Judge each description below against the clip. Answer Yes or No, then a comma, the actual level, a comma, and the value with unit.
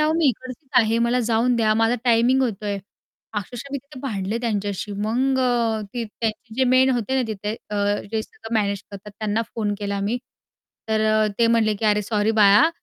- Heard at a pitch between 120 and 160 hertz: No, high, 225 Hz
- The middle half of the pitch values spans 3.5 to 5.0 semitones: No, average, 2.9 semitones